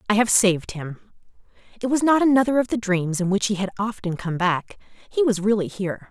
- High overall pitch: Yes, high, 205 Hz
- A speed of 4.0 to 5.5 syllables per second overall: No, 5.9 syllables/s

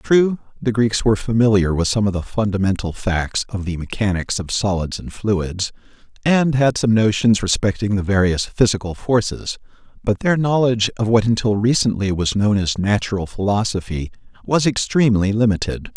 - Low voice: Yes, low, 105 Hz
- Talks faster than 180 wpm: No, average, 160 wpm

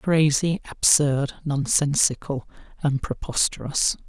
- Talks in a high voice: No, medium, 145 Hz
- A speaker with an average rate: No, slow, 75 wpm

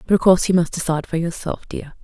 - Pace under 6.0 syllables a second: No, 7.0 syllables/s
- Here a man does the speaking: No, female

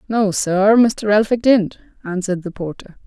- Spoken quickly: No, average, 155 wpm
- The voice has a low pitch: No, high, 205 Hz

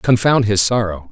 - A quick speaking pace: No, average, 160 wpm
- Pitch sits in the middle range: No, low, 110 Hz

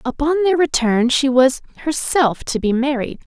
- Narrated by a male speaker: No, female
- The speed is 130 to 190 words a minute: Yes, average, 160 wpm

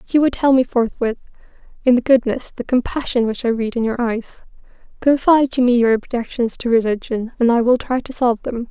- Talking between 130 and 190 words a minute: No, fast, 205 wpm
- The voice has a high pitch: Yes, high, 240 Hz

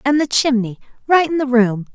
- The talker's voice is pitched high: Yes, very high, 255 Hz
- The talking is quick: Yes, fast, 215 wpm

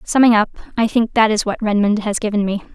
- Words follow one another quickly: Yes, fast, 240 wpm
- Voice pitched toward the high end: Yes, high, 215 Hz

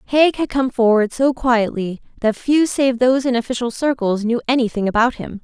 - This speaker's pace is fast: No, average, 190 wpm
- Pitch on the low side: No, high, 245 Hz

